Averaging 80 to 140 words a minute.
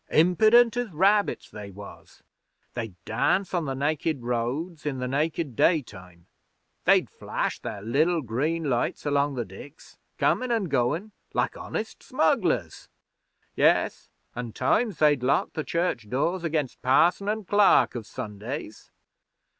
Yes: slow, 135 wpm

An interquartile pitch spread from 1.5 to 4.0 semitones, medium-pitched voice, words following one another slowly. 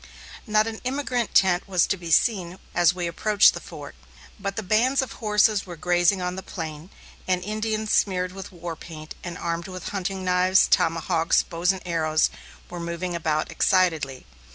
No: average, 3.1 semitones; medium, 180 Hz; average, 170 wpm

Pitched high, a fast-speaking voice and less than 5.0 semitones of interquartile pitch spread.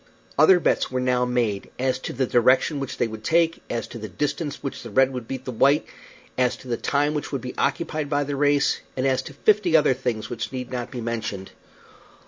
No: low, 130 Hz; fast, 230 wpm; average, 3.0 semitones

